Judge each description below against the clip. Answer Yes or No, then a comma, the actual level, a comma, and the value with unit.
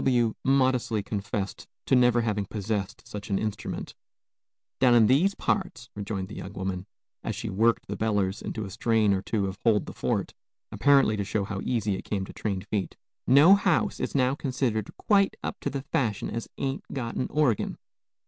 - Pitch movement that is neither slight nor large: Yes, average, 4.2 semitones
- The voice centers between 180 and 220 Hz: No, low, 110 Hz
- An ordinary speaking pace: Yes, average, 185 wpm